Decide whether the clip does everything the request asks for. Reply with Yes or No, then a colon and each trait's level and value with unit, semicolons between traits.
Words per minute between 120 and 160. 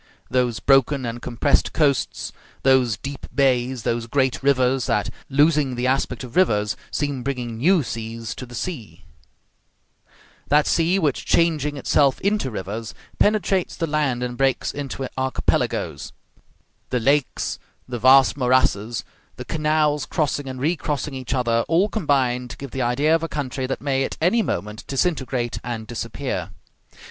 Yes: average, 150 wpm